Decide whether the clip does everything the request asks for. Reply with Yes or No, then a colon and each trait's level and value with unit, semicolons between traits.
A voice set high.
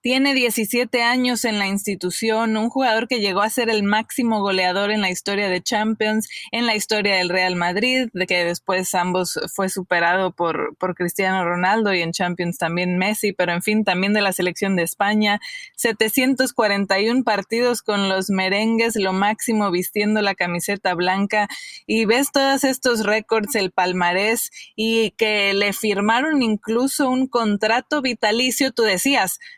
Yes: high, 210 Hz